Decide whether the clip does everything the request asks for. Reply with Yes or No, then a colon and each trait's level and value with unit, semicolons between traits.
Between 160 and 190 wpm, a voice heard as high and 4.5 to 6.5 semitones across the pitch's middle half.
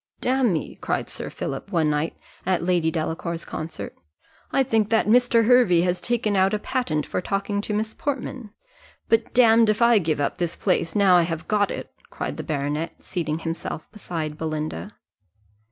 No: average, 170 wpm; medium, 180 Hz; wide, 5.5 semitones